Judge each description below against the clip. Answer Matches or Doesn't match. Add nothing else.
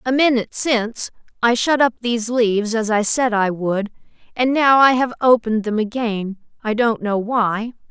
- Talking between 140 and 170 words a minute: Doesn't match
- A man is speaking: Doesn't match